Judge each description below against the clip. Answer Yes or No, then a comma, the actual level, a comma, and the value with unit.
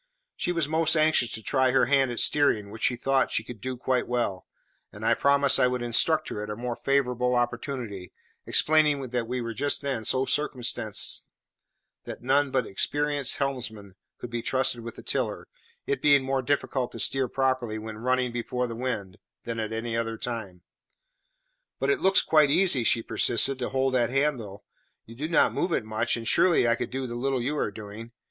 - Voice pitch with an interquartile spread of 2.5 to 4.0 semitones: Yes, average, 3.1 semitones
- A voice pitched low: Yes, low, 125 Hz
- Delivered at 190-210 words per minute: Yes, average, 195 wpm